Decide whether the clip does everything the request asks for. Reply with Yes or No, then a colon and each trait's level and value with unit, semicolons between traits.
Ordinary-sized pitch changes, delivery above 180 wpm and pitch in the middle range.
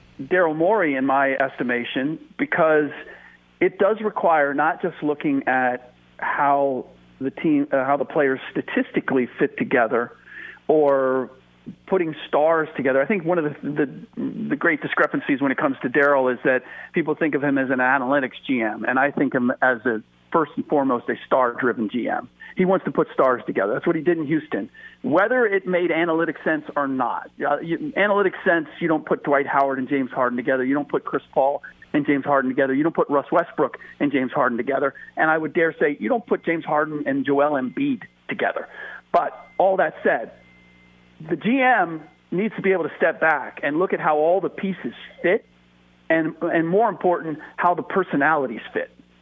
Yes: average, 4.9 semitones; average, 190 wpm; medium, 150 Hz